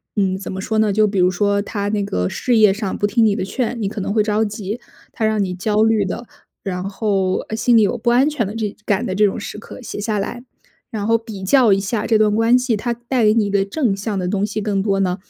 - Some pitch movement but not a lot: No, narrow, 2.3 semitones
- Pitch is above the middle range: Yes, high, 210 Hz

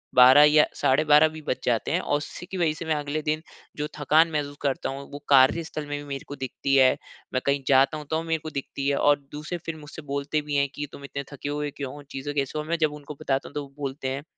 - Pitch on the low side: No, medium, 145 Hz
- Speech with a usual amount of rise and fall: No, narrow, 1.7 semitones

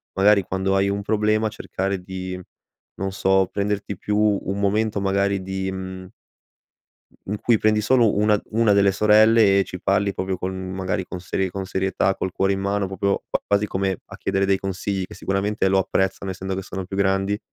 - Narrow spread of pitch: Yes, narrow, 1.3 semitones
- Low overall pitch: Yes, very low, 95 Hz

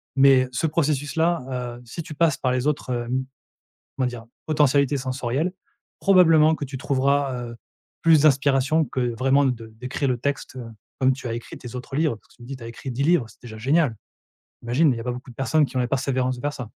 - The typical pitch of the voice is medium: No, low, 130 Hz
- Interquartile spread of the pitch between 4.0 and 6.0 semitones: No, average, 2.8 semitones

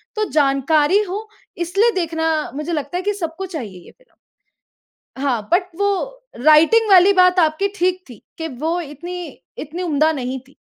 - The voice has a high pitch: Yes, very high, 335 Hz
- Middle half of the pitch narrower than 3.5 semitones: No, average, 4.2 semitones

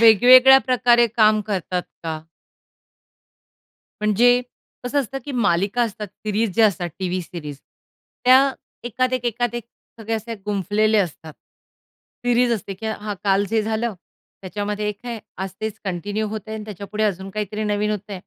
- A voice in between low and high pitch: No, high, 215 Hz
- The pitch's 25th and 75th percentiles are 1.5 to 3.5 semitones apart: Yes, average, 2.9 semitones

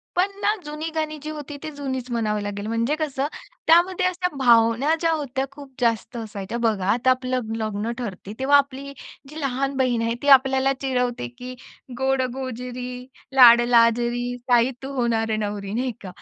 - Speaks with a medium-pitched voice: No, very high, 250 Hz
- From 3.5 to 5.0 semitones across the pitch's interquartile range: No, average, 3.1 semitones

